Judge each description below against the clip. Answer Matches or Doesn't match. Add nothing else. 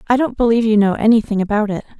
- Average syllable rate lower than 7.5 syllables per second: Doesn't match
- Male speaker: Doesn't match